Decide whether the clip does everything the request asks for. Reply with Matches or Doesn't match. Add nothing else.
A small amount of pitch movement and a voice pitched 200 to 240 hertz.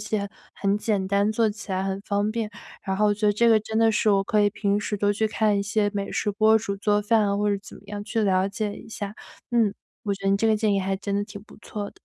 Matches